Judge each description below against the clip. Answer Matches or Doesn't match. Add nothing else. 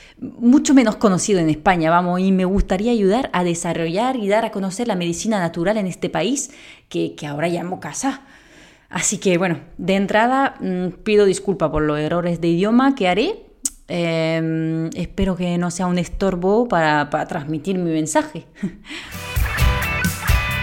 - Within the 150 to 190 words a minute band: Matches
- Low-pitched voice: Doesn't match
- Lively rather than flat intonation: Doesn't match